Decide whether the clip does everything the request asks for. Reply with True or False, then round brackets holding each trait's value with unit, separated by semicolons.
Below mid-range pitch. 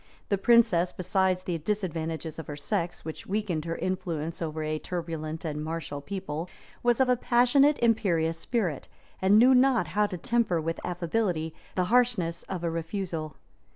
False (175 Hz)